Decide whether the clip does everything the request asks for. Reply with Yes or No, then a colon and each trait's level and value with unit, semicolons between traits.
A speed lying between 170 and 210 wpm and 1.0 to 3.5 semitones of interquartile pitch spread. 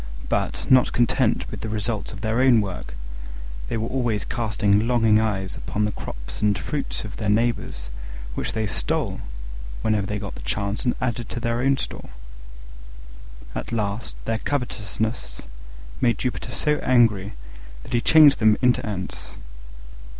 No: average, 155 wpm; average, 2.8 semitones